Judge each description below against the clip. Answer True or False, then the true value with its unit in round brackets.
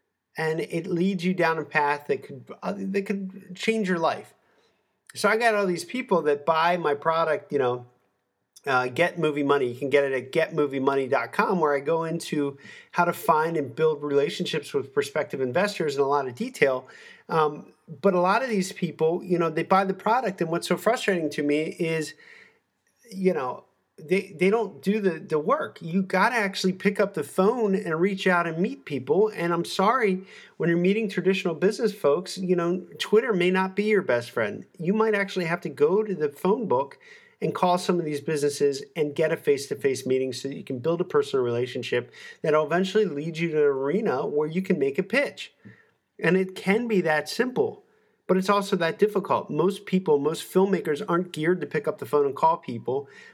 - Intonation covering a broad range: False (4.7 semitones)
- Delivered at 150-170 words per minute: False (205 wpm)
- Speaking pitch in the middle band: True (180 Hz)